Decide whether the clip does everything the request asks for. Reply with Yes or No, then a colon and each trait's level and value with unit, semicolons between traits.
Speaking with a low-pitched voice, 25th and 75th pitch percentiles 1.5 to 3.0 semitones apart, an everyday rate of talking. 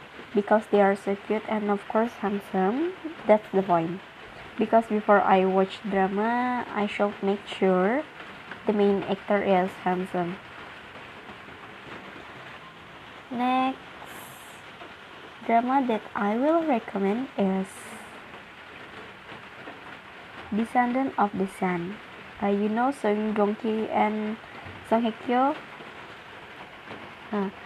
No: high, 210 Hz; average, 2.7 semitones; average, 100 wpm